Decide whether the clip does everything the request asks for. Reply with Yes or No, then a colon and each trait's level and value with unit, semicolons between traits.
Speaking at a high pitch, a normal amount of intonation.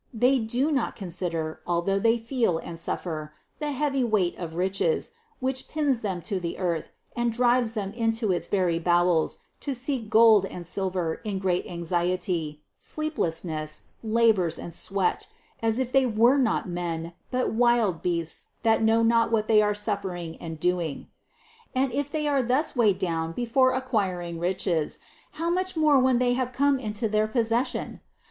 No: high, 215 Hz; wide, 5.9 semitones